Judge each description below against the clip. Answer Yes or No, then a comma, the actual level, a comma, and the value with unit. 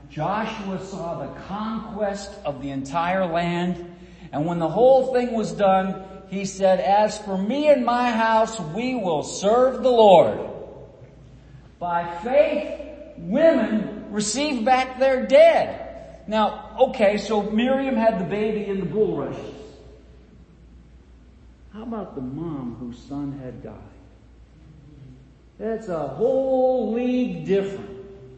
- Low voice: No, high, 200 Hz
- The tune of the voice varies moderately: No, wide, 7.0 semitones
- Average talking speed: No, slow, 125 wpm